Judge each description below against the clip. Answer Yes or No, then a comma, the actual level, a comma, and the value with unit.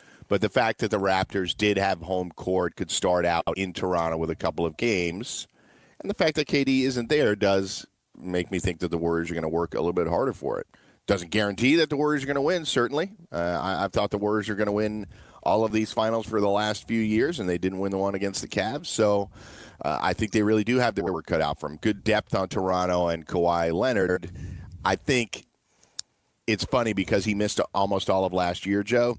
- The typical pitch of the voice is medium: No, low, 100 Hz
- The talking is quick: Yes, fast, 235 wpm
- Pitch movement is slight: No, average, 3.5 semitones